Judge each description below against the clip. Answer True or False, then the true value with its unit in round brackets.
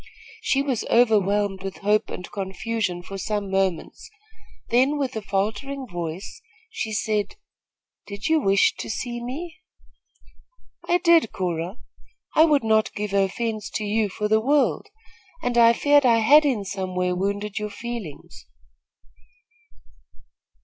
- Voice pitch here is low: False (215 Hz)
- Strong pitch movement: False (4.1 semitones)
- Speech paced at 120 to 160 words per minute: True (135 wpm)